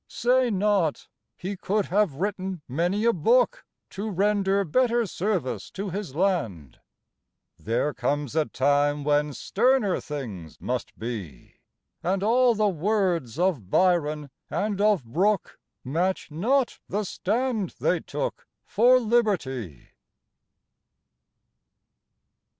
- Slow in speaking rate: Yes, slow, 110 wpm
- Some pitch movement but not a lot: No, wide, 6.4 semitones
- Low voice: No, medium, 185 Hz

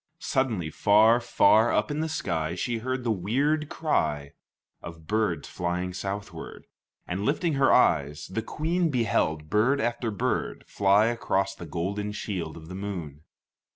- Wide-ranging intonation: Yes, wide, 5.8 semitones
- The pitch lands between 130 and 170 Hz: No, low, 105 Hz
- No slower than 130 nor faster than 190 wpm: Yes, average, 150 wpm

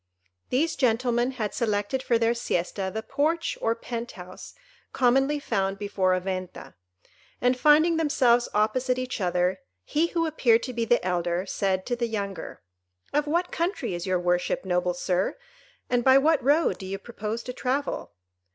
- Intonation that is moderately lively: No, wide, 5.8 semitones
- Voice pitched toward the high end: Yes, high, 235 Hz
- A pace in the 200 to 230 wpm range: No, average, 160 wpm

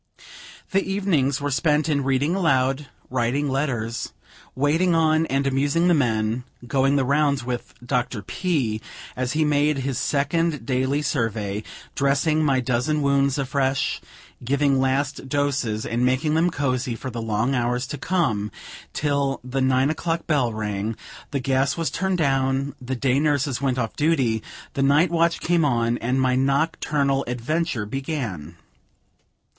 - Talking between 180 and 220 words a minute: No, average, 150 wpm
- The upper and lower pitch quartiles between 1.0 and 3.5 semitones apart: Yes, average, 3.1 semitones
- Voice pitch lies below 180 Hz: Yes, low, 135 Hz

